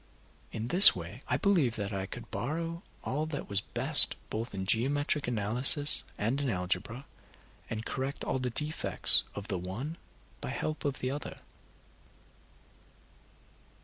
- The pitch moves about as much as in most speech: No, wide, 5.9 semitones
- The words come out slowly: No, average, 145 wpm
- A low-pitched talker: Yes, low, 125 Hz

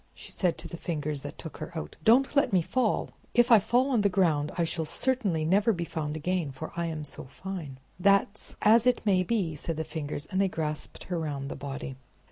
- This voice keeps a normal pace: No, fast, 225 wpm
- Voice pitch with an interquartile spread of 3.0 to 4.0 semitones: No, average, 5.2 semitones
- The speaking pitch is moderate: Yes, medium, 170 Hz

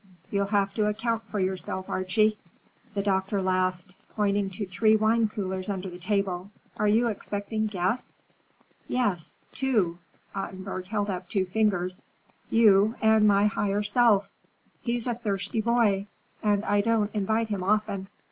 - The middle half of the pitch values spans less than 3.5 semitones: Yes, narrow, 2.4 semitones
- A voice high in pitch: Yes, high, 205 Hz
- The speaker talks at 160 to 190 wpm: No, average, 140 wpm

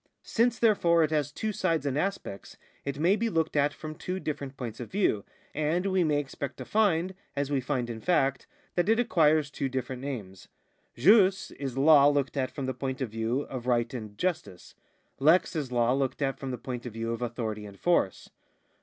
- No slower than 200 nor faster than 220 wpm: Yes, fast, 205 wpm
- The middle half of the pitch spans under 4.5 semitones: No, average, 5.3 semitones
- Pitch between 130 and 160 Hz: Yes, medium, 140 Hz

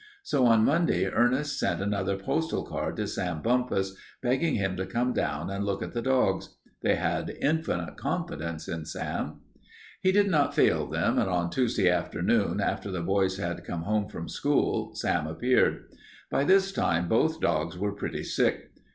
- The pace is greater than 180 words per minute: No, average, 170 wpm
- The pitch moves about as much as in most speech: No, wide, 6.4 semitones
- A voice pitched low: Yes, low, 100 Hz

